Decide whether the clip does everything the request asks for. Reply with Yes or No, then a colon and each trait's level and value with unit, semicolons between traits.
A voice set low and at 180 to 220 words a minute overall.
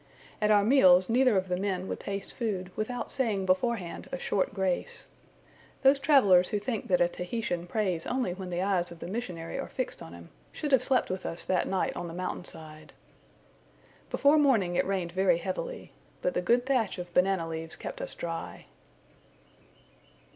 No: high, 190 Hz; average, 185 wpm